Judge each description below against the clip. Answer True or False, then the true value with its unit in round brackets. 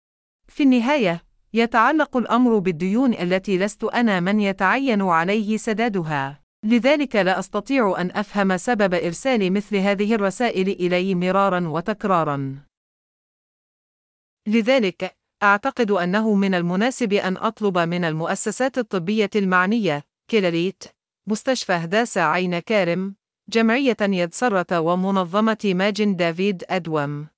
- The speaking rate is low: True (105 wpm)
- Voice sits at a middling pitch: False (200 Hz)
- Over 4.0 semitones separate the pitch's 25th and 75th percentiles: False (3.7 semitones)